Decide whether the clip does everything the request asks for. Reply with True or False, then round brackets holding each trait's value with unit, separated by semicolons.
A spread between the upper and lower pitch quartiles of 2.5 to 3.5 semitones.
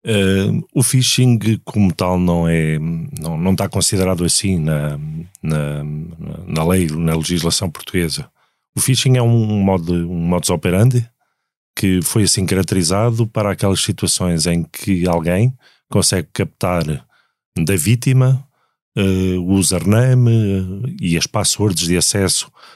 False (4.6 semitones)